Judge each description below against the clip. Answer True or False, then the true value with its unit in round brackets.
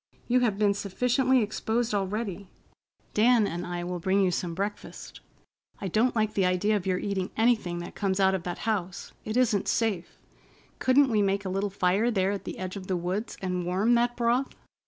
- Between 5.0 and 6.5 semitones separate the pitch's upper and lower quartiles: False (3.4 semitones)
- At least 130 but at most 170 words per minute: False (200 wpm)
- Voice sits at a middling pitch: False (200 Hz)